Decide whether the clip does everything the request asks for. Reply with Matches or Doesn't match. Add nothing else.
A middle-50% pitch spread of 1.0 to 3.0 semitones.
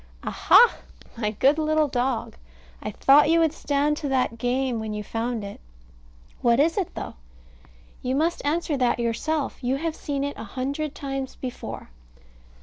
Doesn't match